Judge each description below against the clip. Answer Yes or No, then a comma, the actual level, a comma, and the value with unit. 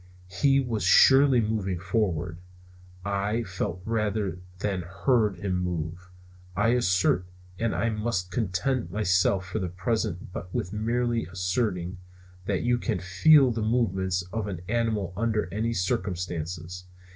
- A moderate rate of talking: No, slow, 130 wpm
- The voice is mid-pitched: No, low, 100 Hz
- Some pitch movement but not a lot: Yes, average, 4.0 semitones